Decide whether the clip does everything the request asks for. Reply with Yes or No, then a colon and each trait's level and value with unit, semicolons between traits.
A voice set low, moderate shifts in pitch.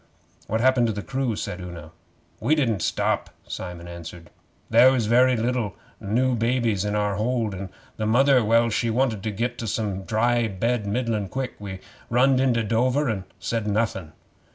Yes: low, 115 Hz; average, 3.4 semitones